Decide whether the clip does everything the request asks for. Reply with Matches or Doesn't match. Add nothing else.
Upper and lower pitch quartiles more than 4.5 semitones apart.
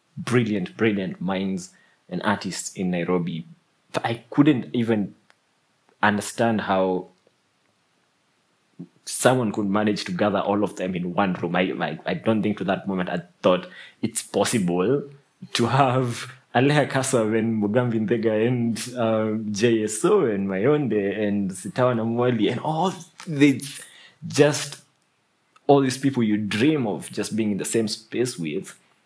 Doesn't match